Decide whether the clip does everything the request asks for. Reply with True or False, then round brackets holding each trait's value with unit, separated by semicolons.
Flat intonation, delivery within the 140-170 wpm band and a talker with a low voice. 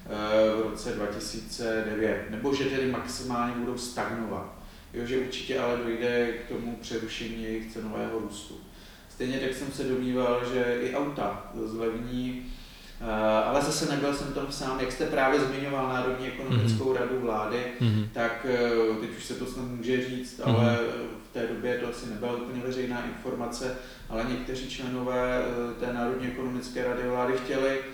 True (2.0 semitones; 150 wpm; 120 Hz)